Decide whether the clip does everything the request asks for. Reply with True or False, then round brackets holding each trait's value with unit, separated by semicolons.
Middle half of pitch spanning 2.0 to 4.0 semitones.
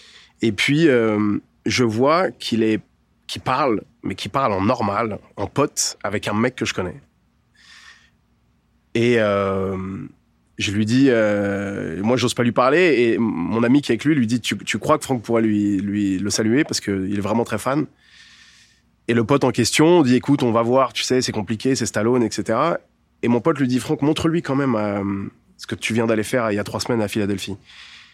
True (3.5 semitones)